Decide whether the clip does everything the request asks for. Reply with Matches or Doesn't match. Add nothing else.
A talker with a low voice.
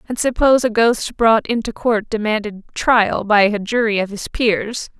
Doesn't match